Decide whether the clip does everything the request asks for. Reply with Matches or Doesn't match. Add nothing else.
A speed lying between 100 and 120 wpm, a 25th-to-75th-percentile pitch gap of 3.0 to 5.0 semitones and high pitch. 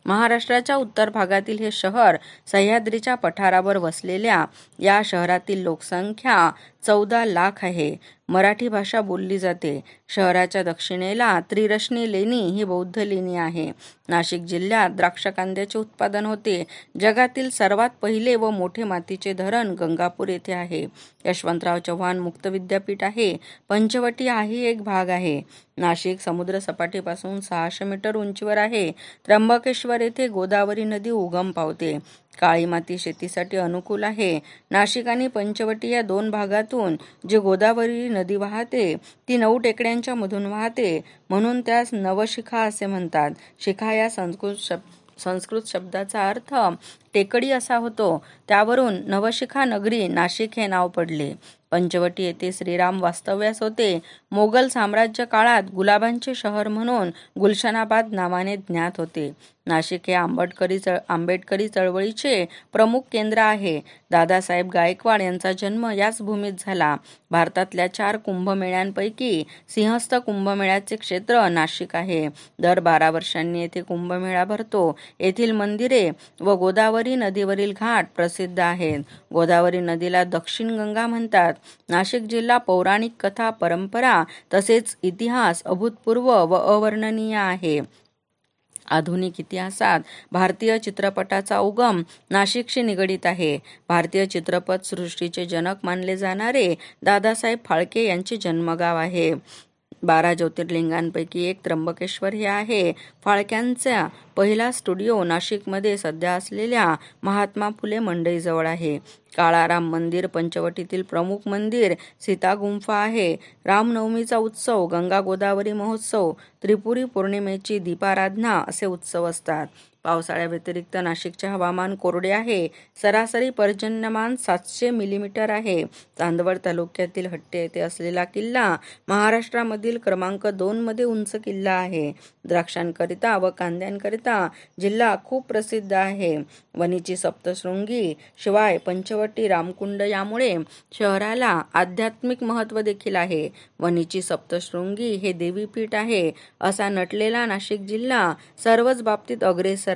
Matches